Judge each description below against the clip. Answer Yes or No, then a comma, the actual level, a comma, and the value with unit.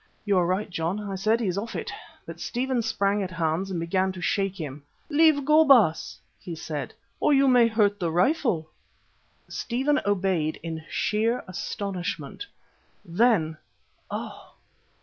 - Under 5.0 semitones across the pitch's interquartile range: No, wide, 5.4 semitones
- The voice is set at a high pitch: Yes, high, 195 Hz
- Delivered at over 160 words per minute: No, average, 150 wpm